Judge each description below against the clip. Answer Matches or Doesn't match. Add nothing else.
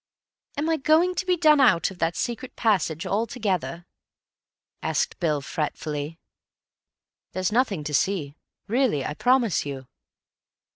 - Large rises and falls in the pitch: Matches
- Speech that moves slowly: Matches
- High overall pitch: Matches